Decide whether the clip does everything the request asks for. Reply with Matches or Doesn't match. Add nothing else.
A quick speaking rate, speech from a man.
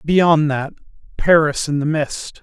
Doesn't match